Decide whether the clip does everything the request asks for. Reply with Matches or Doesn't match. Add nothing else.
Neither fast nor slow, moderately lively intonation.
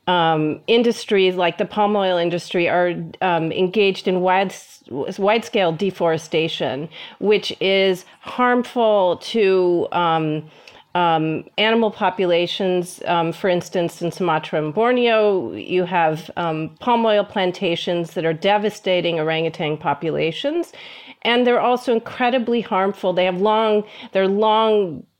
Doesn't match